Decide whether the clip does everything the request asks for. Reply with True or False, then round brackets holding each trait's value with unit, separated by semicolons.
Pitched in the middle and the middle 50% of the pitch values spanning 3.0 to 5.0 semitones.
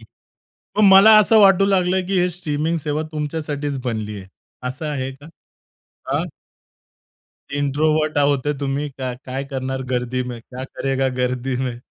True (145 Hz; 3.6 semitones)